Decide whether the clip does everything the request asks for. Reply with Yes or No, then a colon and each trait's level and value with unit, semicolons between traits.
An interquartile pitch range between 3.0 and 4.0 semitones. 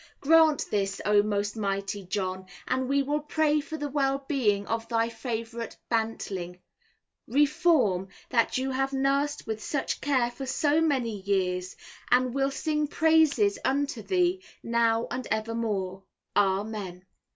No: wide, 5.6 semitones